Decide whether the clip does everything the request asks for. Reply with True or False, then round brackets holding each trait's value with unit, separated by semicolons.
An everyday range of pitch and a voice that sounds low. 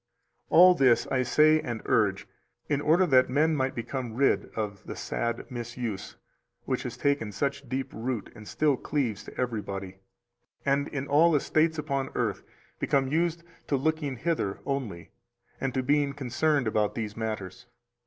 True (4.6 semitones; 130 Hz)